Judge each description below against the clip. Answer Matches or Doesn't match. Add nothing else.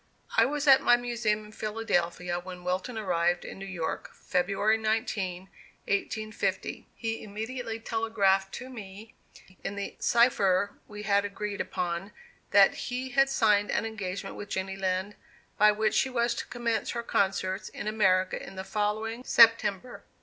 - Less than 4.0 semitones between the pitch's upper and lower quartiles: Matches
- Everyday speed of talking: Matches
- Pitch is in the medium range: Doesn't match